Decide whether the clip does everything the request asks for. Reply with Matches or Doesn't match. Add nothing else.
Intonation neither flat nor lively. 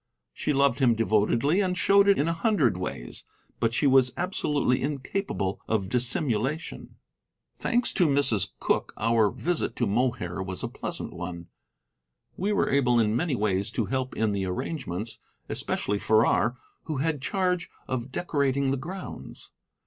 Doesn't match